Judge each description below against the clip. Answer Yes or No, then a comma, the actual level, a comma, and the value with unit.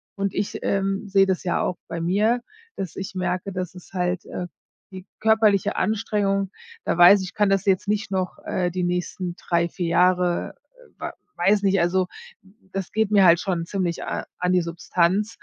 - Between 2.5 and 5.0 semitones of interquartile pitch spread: No, narrow, 1.9 semitones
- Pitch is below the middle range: No, medium, 185 Hz